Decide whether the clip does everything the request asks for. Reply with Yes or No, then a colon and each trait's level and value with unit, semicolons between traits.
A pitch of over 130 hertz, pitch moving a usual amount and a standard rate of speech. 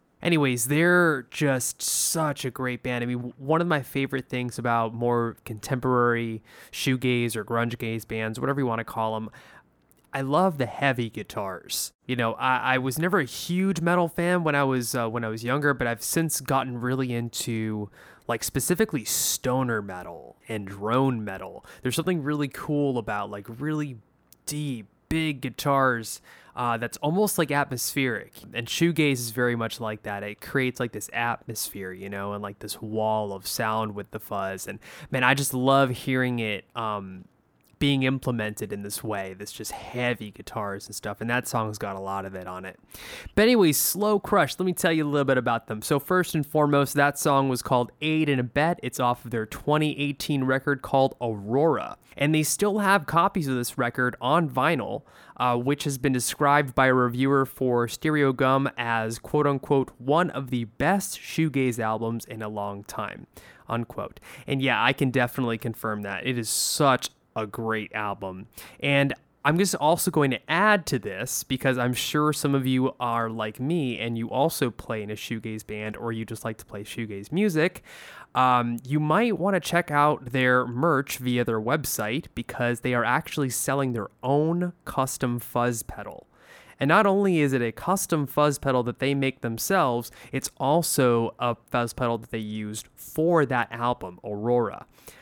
No: low, 125 Hz; average, 4.1 semitones; average, 185 wpm